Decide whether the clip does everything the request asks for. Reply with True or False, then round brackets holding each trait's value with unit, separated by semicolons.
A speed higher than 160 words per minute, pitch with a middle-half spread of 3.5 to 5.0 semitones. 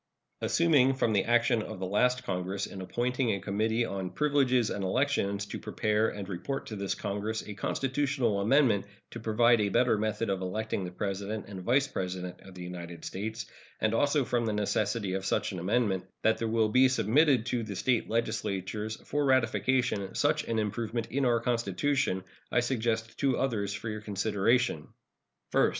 True (175 wpm; 3.8 semitones)